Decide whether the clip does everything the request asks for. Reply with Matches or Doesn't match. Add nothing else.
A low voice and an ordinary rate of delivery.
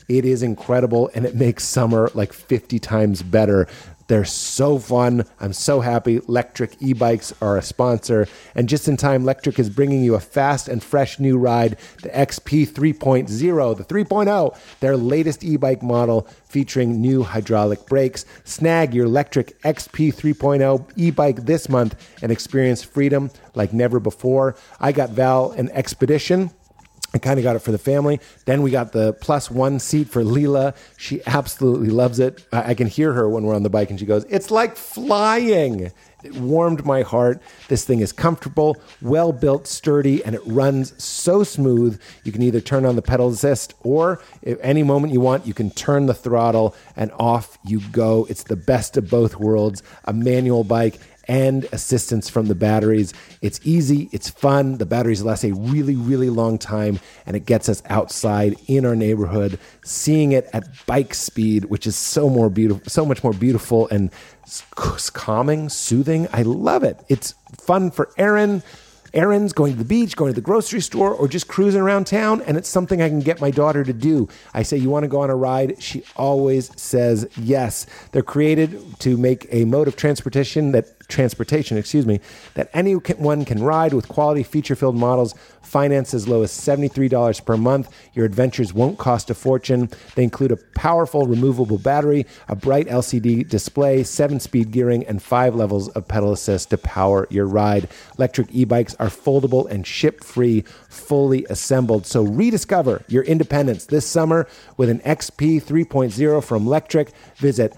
Matches